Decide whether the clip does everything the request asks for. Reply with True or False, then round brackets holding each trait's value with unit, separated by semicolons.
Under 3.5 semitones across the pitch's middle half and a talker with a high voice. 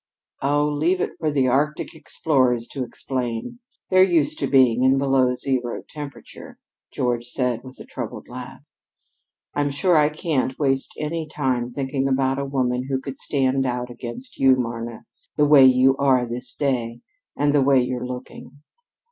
False (2.6 semitones; 135 Hz)